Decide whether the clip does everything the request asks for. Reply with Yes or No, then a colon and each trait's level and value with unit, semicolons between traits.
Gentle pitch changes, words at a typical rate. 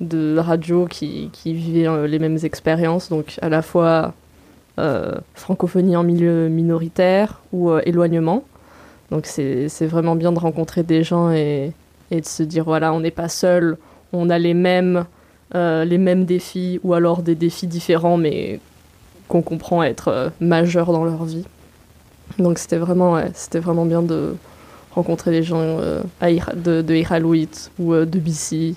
Yes: narrow, 1.3 semitones; average, 170 wpm